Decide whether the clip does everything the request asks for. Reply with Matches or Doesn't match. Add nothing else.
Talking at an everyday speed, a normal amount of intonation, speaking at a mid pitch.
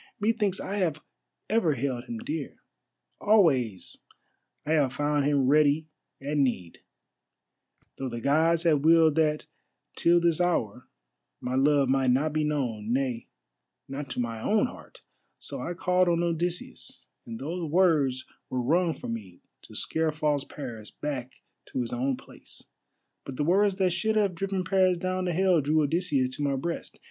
Matches